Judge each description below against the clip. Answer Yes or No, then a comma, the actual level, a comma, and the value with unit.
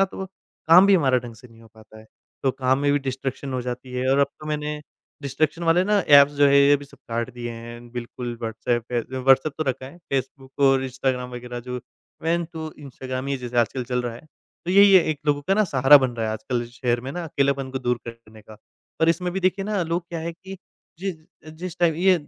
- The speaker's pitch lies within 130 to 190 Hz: Yes, low, 135 Hz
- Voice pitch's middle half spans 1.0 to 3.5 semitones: No, average, 4.6 semitones